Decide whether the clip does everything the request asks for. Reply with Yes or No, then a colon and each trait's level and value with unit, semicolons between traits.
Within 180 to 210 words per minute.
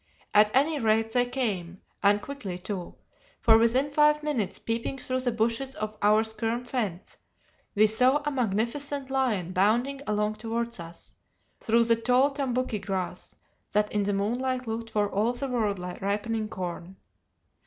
No: average, 155 wpm